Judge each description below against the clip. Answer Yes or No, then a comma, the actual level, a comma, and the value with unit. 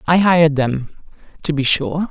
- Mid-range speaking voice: Yes, medium, 155 Hz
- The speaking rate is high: No, average, 170 wpm